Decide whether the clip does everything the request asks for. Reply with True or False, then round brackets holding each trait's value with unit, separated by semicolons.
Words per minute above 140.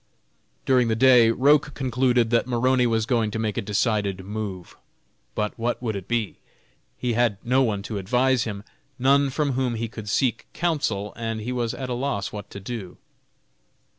True (180 wpm)